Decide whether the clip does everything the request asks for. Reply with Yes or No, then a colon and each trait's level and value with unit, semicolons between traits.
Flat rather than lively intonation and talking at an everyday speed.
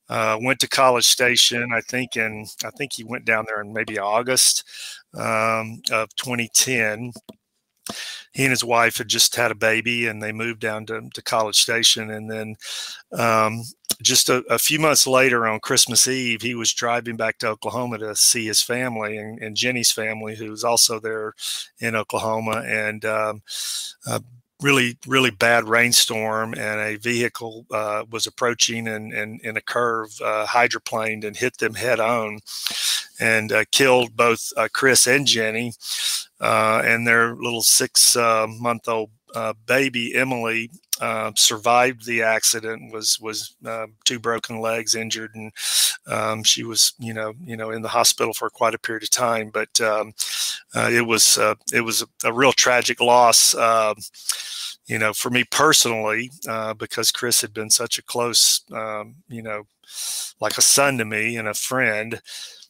Yes: narrow, 1.6 semitones; average, 170 wpm